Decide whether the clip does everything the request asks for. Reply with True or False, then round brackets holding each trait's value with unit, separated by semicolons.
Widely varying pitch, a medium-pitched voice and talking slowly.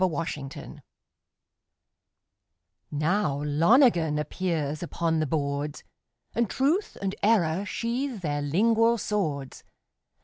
True (6.9 semitones; 165 Hz; 95 wpm)